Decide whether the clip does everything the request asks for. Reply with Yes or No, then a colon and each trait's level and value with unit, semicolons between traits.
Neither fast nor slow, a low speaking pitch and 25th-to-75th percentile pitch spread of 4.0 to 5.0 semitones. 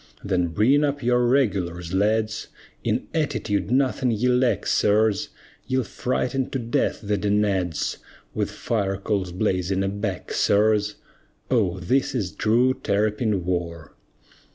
No: slow, 125 wpm; low, 105 Hz; average, 4.3 semitones